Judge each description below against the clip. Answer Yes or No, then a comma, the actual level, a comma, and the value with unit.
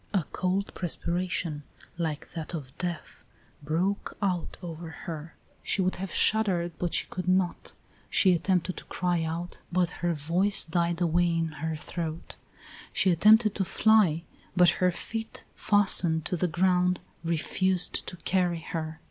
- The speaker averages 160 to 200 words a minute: No, average, 150 wpm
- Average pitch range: No, narrow, 2.1 semitones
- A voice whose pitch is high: No, medium, 175 Hz